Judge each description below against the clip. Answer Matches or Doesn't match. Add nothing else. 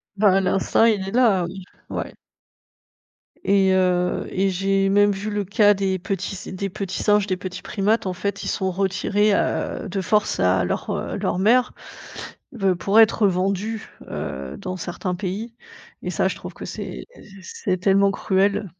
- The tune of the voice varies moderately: Doesn't match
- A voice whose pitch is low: Doesn't match